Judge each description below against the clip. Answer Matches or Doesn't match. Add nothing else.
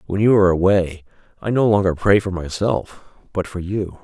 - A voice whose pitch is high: Doesn't match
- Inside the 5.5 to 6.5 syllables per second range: Doesn't match